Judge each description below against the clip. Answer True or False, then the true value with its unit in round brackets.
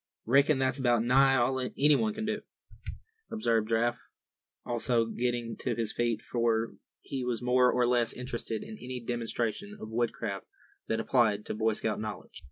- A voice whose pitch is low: True (120 Hz)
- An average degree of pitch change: False (2.2 semitones)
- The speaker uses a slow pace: False (160 wpm)